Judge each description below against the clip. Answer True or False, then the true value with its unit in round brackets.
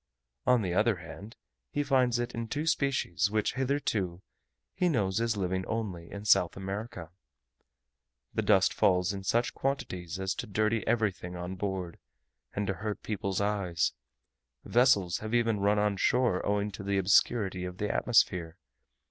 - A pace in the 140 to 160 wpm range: True (155 wpm)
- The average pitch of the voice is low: True (100 Hz)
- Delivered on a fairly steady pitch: False (3.6 semitones)